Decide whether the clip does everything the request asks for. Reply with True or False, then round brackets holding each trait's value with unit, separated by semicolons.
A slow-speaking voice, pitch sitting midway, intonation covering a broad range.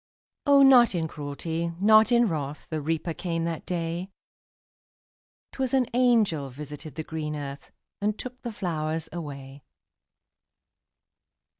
True (125 wpm; 165 Hz; 6.2 semitones)